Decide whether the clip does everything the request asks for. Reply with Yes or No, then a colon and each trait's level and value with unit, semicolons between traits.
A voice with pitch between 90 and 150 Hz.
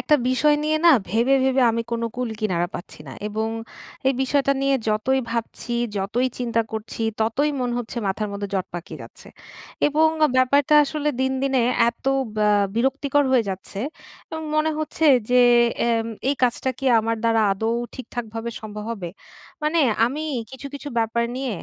No: high, 245 Hz